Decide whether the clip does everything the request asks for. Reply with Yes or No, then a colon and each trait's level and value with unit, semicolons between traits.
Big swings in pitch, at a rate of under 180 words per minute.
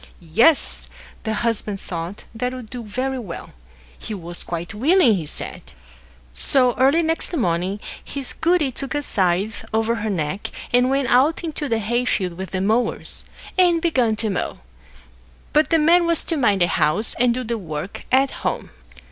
Yes: wide, 5.8 semitones; average, 170 wpm